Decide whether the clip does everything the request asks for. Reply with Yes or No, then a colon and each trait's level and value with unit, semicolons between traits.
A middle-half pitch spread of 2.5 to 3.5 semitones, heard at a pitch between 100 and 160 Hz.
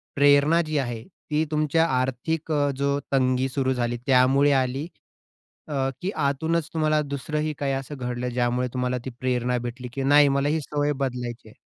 Yes: average, 2.9 semitones; medium, 140 Hz